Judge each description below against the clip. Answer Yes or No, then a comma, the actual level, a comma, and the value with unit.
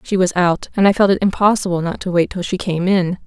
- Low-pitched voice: No, medium, 185 Hz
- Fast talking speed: Yes, fast, 275 wpm